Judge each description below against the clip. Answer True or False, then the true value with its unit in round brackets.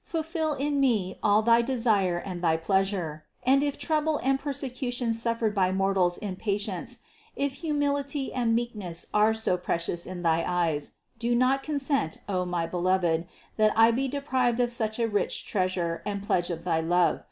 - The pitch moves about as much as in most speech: False (6.5 semitones)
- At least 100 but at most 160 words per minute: False (175 wpm)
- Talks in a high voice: True (215 Hz)